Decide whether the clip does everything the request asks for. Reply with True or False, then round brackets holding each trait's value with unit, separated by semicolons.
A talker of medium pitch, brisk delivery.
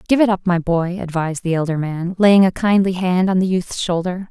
True (180 Hz; 235 wpm)